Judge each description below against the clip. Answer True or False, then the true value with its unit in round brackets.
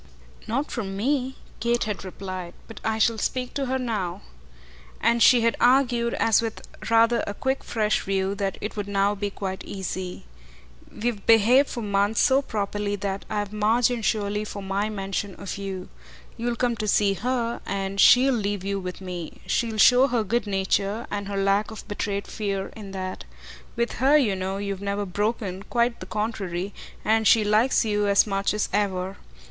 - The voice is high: True (210 Hz)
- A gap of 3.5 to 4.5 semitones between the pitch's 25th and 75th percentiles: False (3.0 semitones)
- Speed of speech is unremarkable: True (180 wpm)